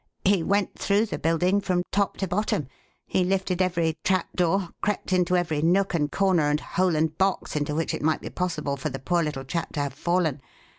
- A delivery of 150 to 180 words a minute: No, fast, 205 wpm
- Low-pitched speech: No, medium, 175 Hz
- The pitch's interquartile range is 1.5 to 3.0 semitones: No, average, 3.4 semitones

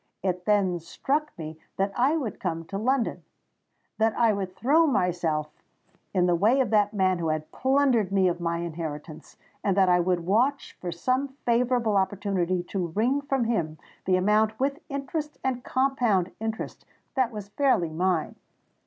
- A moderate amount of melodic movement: No, wide, 6.2 semitones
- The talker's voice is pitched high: Yes, high, 200 Hz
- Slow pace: No, average, 160 wpm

